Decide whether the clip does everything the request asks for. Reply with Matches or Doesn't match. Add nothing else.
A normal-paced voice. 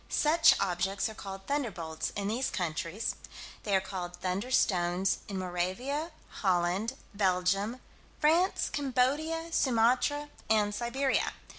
Doesn't match